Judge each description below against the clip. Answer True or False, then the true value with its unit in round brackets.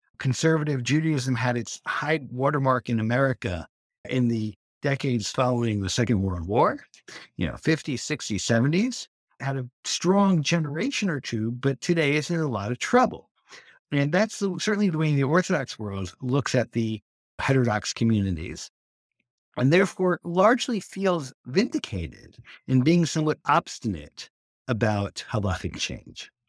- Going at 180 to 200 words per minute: False (140 wpm)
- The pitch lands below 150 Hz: True (135 Hz)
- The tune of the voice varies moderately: False (6.4 semitones)